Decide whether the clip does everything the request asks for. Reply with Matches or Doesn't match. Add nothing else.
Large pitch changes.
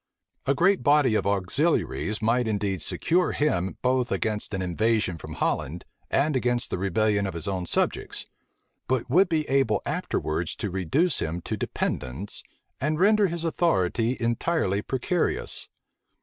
Matches